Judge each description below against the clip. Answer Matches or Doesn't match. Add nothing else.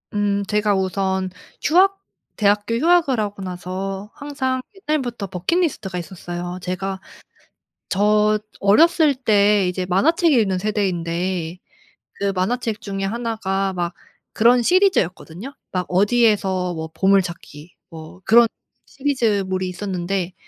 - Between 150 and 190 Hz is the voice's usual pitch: Doesn't match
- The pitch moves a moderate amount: Matches